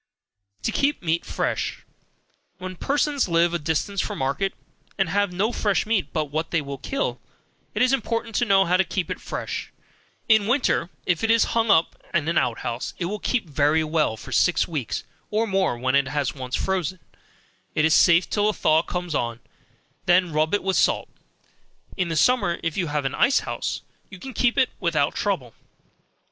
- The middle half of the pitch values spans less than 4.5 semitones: No, average, 5.0 semitones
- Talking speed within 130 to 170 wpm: No, average, 190 wpm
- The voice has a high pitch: No, medium, 175 Hz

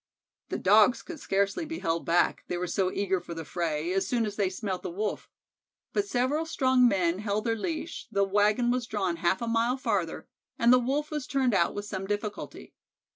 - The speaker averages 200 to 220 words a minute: Yes, fast, 205 wpm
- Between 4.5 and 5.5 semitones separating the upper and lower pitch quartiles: Yes, average, 4.9 semitones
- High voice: Yes, high, 210 Hz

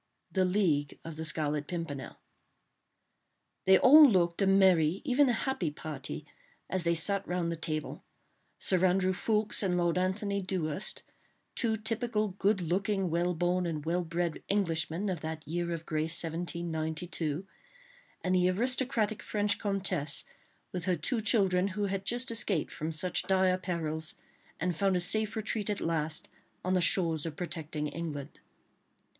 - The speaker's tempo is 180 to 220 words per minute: No, average, 150 wpm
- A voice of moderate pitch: Yes, medium, 180 Hz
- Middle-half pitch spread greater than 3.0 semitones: Yes, average, 3.6 semitones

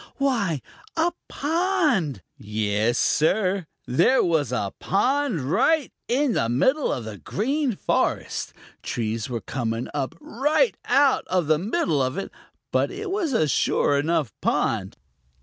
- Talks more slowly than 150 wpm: Yes, slow, 135 wpm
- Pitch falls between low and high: Yes, medium, 180 Hz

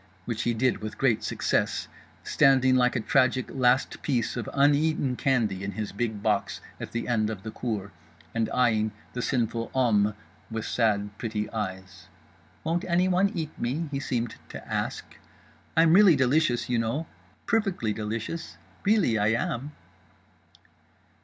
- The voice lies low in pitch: Yes, low, 120 Hz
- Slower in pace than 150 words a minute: Yes, average, 140 wpm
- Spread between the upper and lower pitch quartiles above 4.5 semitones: No, average, 4.2 semitones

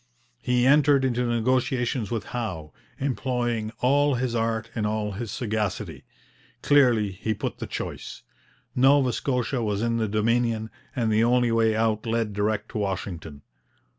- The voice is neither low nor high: No, low, 115 Hz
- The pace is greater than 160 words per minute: No, average, 145 wpm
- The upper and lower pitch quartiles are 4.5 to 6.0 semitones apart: No, narrow, 2.6 semitones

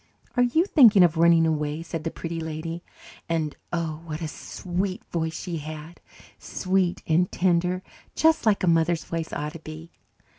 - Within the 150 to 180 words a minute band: Yes, average, 170 wpm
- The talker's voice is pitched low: No, medium, 165 Hz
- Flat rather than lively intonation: Yes, narrow, 2.2 semitones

